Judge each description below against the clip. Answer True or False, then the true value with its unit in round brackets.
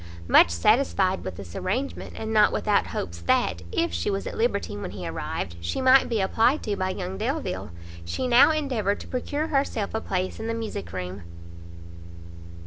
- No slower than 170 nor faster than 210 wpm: True (180 wpm)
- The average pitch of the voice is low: False (205 Hz)